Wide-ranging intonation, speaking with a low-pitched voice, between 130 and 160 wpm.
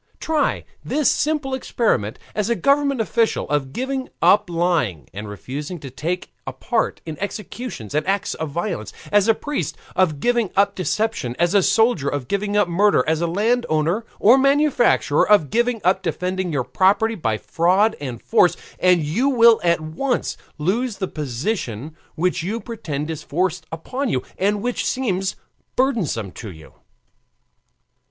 No: wide, 6.9 semitones; medium, 185 Hz; average, 155 wpm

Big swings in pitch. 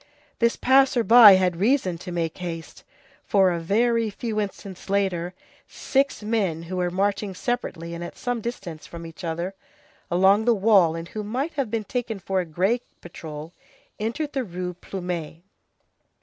No: average, 4.8 semitones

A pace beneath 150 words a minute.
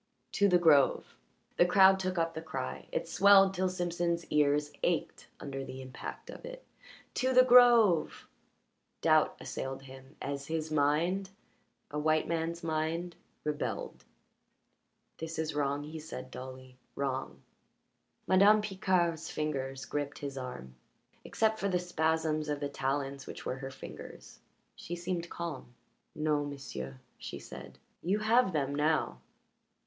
Yes: average, 140 wpm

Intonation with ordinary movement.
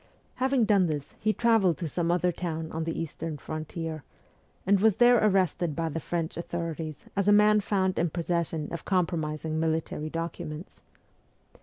Yes: average, 3.4 semitones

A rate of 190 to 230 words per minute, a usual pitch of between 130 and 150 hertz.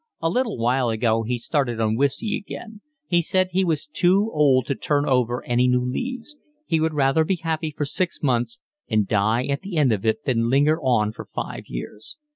Yes: fast, 205 wpm; medium, 140 Hz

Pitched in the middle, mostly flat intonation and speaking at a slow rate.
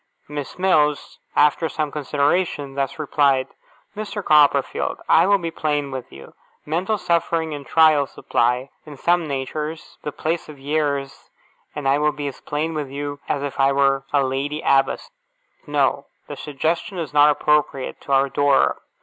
No: medium, 145 Hz; narrow, 2.3 semitones; average, 160 wpm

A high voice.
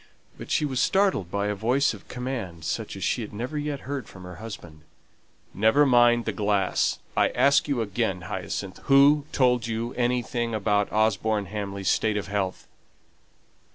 No: low, 110 Hz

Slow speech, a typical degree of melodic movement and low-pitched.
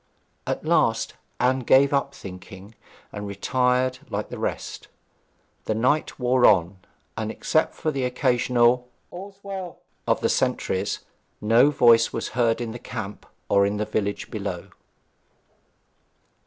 Yes: slow, 130 wpm; average, 3.6 semitones; low, 120 Hz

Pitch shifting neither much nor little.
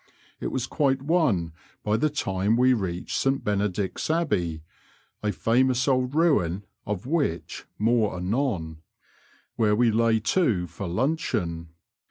No: wide, 6.4 semitones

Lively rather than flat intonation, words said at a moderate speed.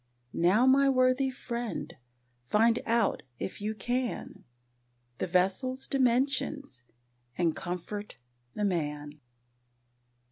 No: wide, 6.3 semitones; slow, 95 wpm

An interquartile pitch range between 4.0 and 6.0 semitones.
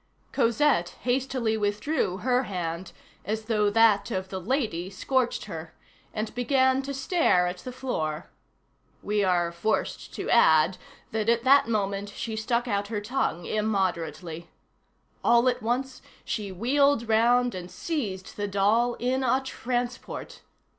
Yes: average, 4.7 semitones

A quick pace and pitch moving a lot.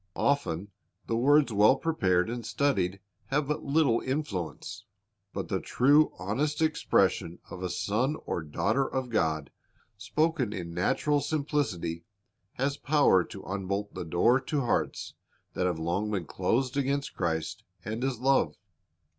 No: average, 140 wpm; wide, 7.3 semitones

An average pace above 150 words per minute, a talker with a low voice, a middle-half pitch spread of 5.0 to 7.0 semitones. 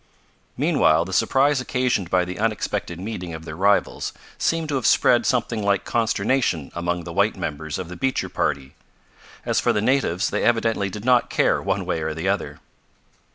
Yes: average, 180 wpm; low, 100 Hz; wide, 5.6 semitones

